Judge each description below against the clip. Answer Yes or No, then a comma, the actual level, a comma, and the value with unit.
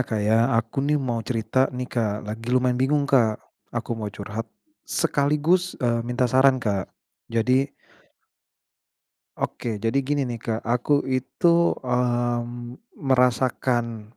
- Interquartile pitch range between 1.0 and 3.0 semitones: Yes, average, 2.7 semitones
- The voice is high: No, low, 125 Hz